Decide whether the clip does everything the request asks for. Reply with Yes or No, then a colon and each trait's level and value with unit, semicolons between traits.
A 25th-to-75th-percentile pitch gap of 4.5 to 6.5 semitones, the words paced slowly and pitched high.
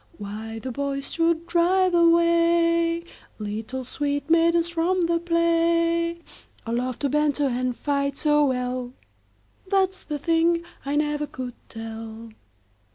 Yes: average, 4.9 semitones; slow, 130 wpm; very high, 300 Hz